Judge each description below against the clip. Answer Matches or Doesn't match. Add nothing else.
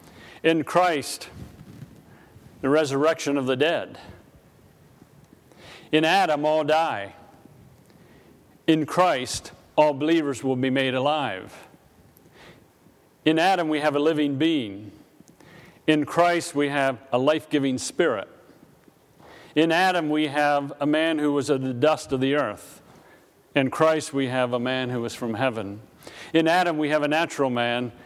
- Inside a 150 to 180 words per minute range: Doesn't match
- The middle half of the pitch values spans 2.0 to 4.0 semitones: Matches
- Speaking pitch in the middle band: Matches